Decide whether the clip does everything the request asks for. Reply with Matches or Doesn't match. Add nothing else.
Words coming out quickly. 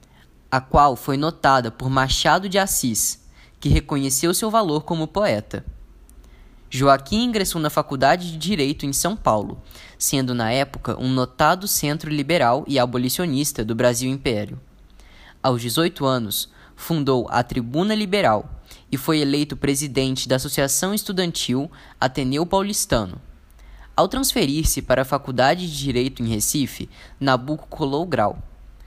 Doesn't match